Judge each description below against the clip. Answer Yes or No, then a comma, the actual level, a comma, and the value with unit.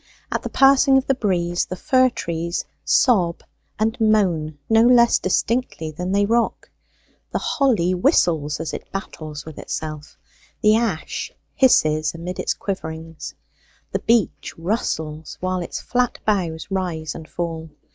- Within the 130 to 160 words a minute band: Yes, average, 140 wpm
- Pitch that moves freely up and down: Yes, wide, 5.7 semitones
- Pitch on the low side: No, medium, 180 Hz